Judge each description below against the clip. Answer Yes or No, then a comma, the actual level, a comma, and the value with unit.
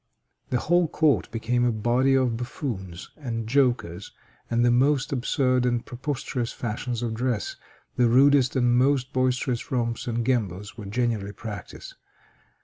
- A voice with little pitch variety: Yes, narrow, 2.2 semitones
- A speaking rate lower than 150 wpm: Yes, average, 140 wpm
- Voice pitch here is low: Yes, low, 120 Hz